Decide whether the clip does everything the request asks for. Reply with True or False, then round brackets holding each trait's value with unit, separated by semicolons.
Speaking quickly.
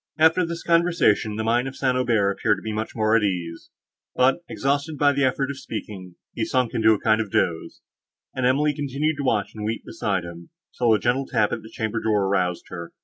True (220 wpm)